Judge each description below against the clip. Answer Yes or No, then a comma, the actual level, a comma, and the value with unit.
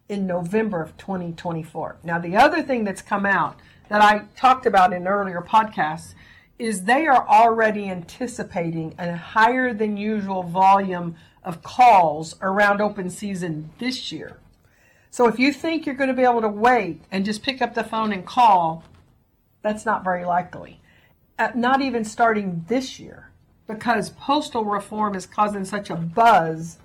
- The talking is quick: No, average, 160 wpm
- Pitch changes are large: No, average, 4.5 semitones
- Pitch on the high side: Yes, high, 210 Hz